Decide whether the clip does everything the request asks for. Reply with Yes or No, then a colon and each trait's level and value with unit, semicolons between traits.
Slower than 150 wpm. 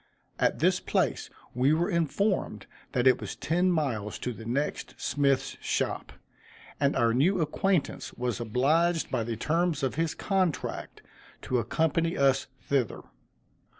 Yes: average, 140 wpm